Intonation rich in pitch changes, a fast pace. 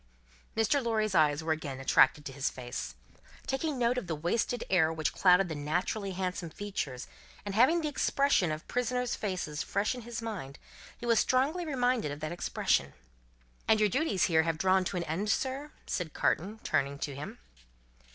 No: wide, 7.3 semitones; average, 180 wpm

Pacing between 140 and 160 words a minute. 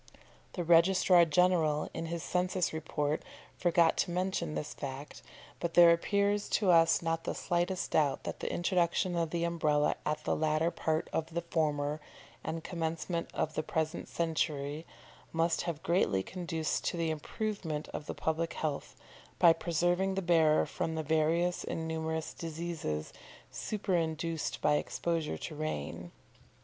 Yes: average, 150 wpm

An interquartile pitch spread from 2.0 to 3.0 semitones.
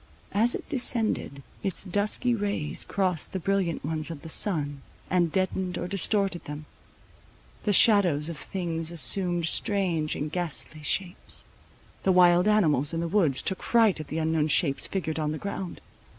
No: average, 4.1 semitones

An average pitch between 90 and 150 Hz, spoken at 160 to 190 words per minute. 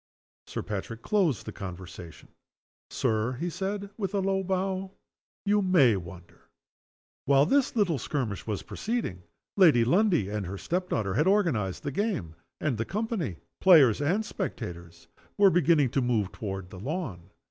No: medium, 140 Hz; average, 150 wpm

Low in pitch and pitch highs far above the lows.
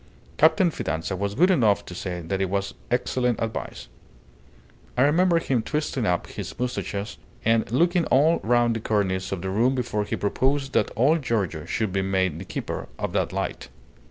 Yes: low, 115 Hz; wide, 5.8 semitones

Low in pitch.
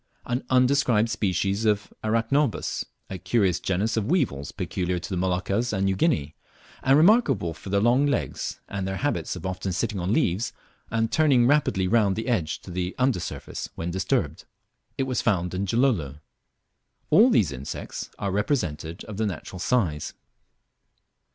Yes: low, 100 Hz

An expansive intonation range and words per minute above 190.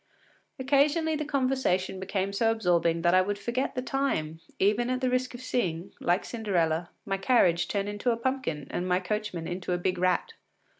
No: wide, 6.1 semitones; average, 185 wpm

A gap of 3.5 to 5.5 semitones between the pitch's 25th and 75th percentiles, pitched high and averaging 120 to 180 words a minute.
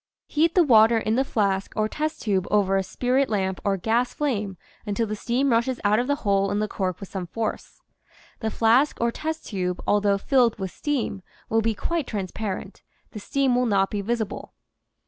No: average, 3.9 semitones; high, 220 Hz; average, 200 wpm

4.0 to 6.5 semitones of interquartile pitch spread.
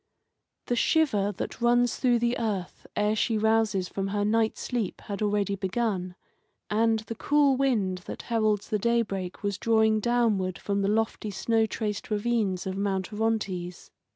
No: narrow, 2.5 semitones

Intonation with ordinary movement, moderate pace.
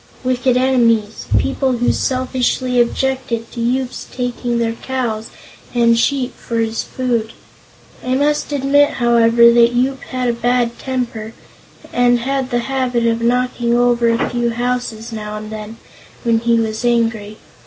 No: narrow, 1.7 semitones; average, 145 wpm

